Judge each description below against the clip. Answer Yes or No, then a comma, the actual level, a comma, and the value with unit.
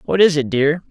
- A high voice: No, medium, 155 Hz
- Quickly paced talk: Yes, fast, 265 wpm